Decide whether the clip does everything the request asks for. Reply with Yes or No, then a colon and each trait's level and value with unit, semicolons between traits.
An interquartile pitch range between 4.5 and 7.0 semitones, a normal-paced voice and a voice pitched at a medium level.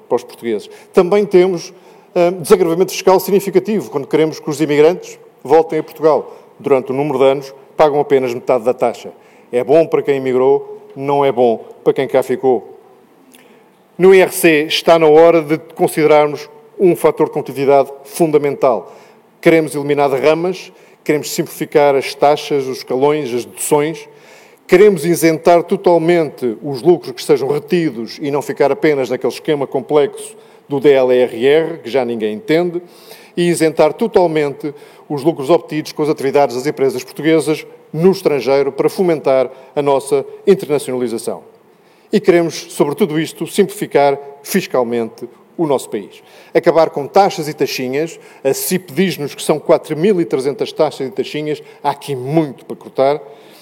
Yes: average, 4.9 semitones; average, 150 wpm; medium, 155 Hz